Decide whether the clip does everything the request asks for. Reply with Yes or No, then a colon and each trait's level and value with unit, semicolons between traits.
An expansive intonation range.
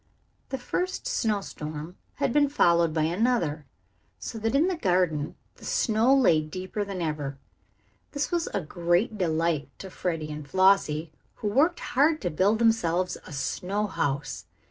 Yes: wide, 6.2 semitones